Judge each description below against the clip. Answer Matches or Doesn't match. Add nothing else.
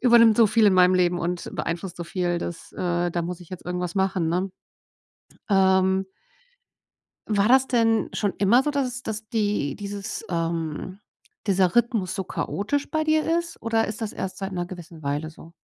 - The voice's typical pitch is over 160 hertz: Matches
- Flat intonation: Doesn't match